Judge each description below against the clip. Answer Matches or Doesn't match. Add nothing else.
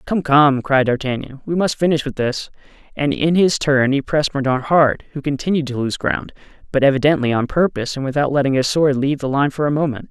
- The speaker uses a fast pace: Matches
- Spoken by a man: Matches